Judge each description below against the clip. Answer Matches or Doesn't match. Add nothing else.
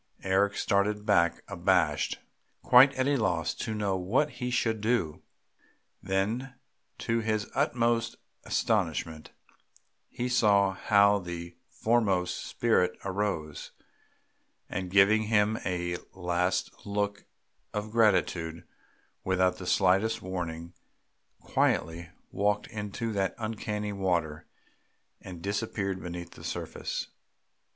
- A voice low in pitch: Matches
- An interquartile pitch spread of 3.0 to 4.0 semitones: Matches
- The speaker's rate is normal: Doesn't match